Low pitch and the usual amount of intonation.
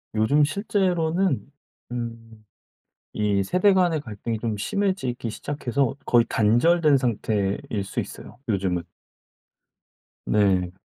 No: low, 120 Hz; wide, 7.3 semitones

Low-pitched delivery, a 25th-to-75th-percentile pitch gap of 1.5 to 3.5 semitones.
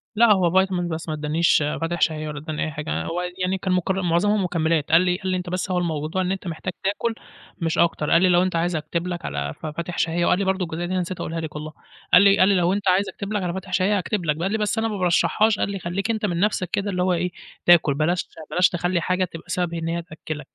No: medium, 175 Hz; narrow, 2.4 semitones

